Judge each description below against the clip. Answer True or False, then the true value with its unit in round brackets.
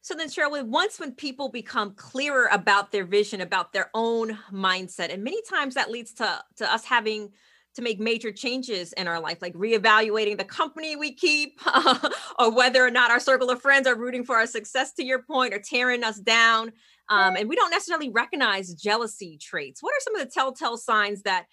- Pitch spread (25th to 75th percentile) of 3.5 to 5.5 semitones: True (4.2 semitones)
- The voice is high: True (235 Hz)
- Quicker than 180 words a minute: True (205 wpm)